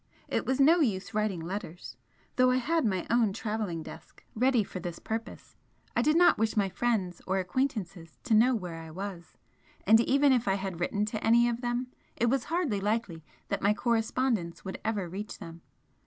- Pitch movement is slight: No, average, 4.5 semitones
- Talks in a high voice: Yes, high, 215 Hz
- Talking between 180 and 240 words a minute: Yes, average, 190 wpm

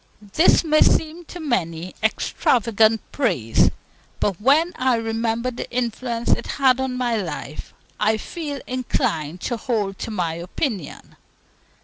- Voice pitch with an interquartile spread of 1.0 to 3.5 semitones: No, average, 4.6 semitones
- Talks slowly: Yes, slow, 130 wpm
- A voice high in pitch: Yes, high, 230 Hz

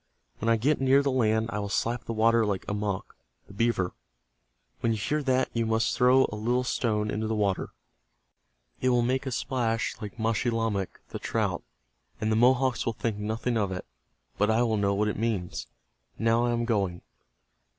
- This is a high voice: No, low, 115 Hz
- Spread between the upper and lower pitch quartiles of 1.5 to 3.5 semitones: Yes, narrow, 2.4 semitones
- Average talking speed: Yes, average, 190 wpm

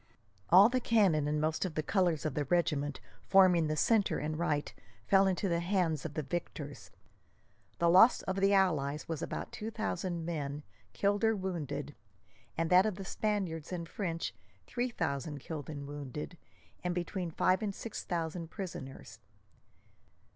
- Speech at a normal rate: Yes, average, 160 wpm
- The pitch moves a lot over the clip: No, average, 4.1 semitones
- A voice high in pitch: No, medium, 170 Hz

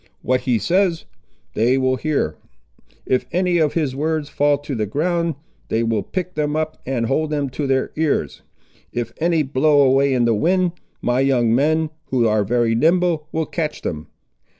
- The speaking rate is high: No, average, 175 wpm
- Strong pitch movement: No, average, 4.4 semitones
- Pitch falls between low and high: Yes, medium, 145 Hz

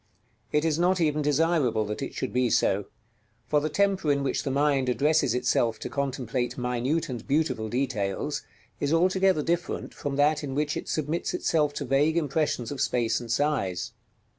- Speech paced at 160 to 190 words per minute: Yes, average, 175 wpm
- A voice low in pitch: No, medium, 145 Hz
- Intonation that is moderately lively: Yes, average, 3.9 semitones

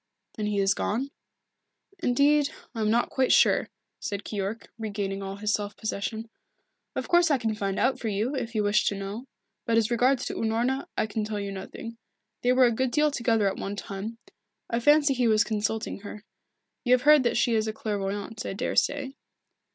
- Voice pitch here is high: Yes, high, 225 Hz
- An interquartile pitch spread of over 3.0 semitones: Yes, average, 3.5 semitones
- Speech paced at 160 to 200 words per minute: Yes, average, 195 wpm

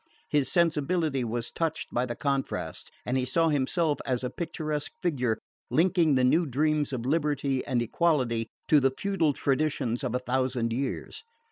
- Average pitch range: Yes, average, 3.7 semitones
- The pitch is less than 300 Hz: Yes, medium, 140 Hz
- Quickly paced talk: No, average, 160 wpm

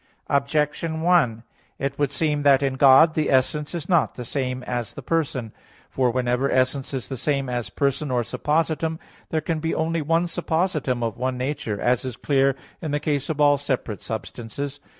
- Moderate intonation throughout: Yes, average, 3.4 semitones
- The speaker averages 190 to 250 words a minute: No, average, 180 wpm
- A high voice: No, medium, 140 Hz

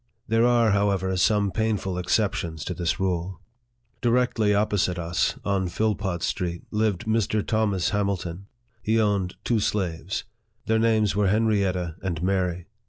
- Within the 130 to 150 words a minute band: Yes, average, 140 wpm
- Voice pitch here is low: Yes, low, 100 Hz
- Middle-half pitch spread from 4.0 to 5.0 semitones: No, average, 3.2 semitones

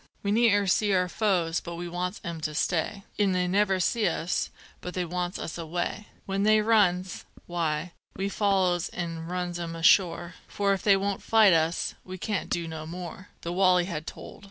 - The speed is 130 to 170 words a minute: No, average, 190 wpm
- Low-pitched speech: No, medium, 180 Hz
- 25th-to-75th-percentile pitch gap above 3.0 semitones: No, narrow, 2.6 semitones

